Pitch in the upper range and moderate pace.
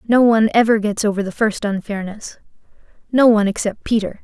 Yes: high, 215 Hz; average, 170 wpm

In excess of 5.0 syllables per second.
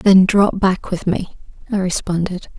No: 4.4 syllables/s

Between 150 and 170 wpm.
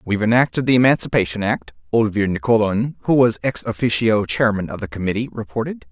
Yes: average, 160 wpm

